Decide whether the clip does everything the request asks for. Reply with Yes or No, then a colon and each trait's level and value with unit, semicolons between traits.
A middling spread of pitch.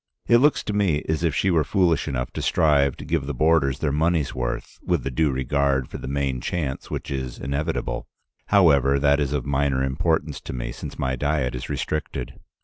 Yes: average, 3.2 semitones